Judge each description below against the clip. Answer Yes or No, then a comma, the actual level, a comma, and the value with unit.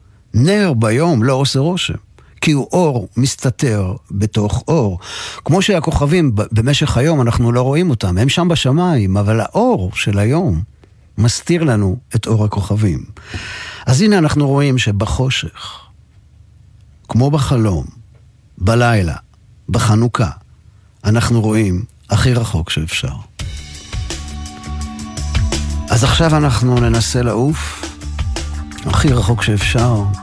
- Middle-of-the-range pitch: No, low, 115 Hz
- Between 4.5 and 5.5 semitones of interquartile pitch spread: Yes, average, 4.9 semitones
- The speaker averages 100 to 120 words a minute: Yes, average, 105 wpm